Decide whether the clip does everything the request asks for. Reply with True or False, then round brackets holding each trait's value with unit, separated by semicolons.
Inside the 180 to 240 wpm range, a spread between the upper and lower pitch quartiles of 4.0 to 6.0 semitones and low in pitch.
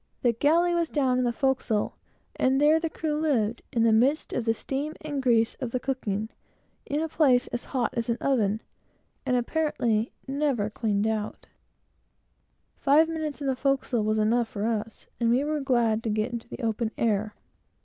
False (190 wpm; 4.3 semitones; 245 Hz)